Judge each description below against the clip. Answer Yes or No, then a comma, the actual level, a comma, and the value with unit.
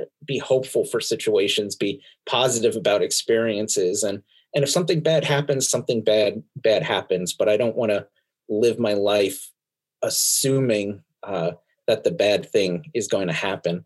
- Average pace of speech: Yes, average, 155 wpm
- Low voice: No, medium, 145 Hz